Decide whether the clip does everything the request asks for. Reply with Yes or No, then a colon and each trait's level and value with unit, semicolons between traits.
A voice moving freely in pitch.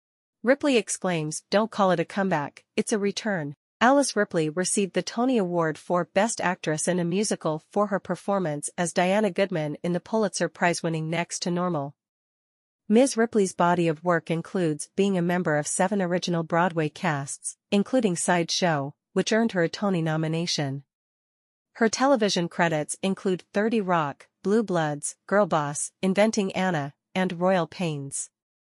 No: average, 3.7 semitones